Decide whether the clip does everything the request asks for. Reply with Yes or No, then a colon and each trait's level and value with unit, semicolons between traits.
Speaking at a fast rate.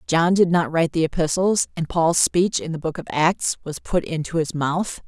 Yes: fast, 225 wpm